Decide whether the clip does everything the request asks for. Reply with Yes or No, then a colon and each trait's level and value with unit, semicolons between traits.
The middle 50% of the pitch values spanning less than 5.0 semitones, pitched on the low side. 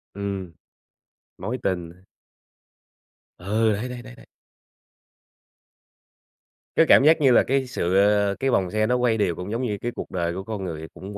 Yes: average, 4.6 semitones; low, 105 Hz